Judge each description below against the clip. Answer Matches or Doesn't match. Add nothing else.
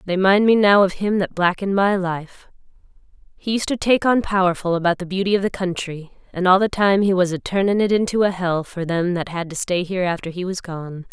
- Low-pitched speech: Doesn't match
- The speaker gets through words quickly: Matches